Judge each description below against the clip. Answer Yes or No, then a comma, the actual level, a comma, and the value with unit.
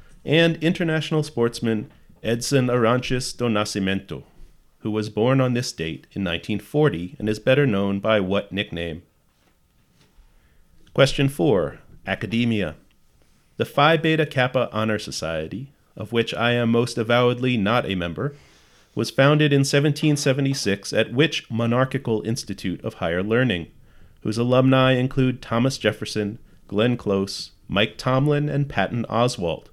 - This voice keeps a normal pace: No, slow, 125 wpm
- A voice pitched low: Yes, low, 115 Hz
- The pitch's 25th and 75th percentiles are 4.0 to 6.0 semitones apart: Yes, average, 4.6 semitones